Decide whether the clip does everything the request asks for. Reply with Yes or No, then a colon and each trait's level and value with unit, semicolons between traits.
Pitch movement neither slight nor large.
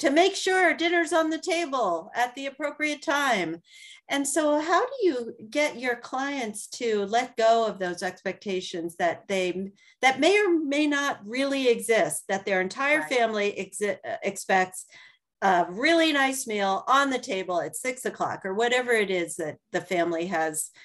No: wide, 7.6 semitones